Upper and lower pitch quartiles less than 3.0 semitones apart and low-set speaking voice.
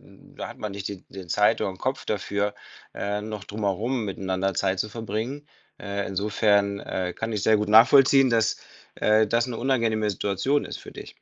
Yes: narrow, 2.4 semitones; low, 105 Hz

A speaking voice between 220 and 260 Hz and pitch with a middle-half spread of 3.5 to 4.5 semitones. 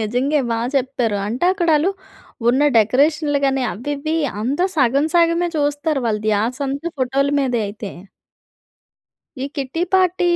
No: very high, 275 Hz; average, 4.1 semitones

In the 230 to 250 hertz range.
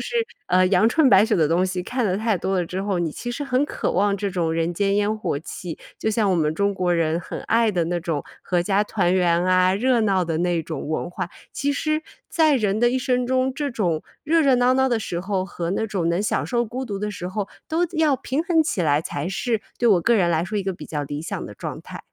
No: high, 195 Hz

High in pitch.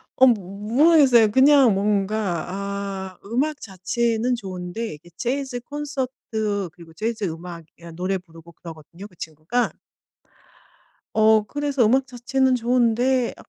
Yes: high, 220 Hz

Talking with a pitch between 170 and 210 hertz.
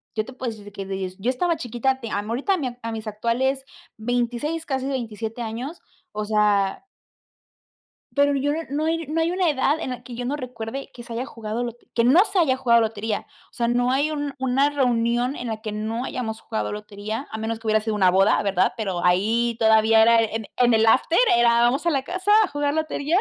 No: high, 240 Hz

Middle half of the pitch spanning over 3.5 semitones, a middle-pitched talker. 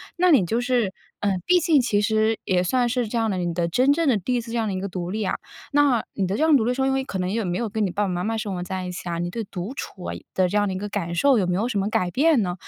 No: average, 5.1 semitones; high, 210 Hz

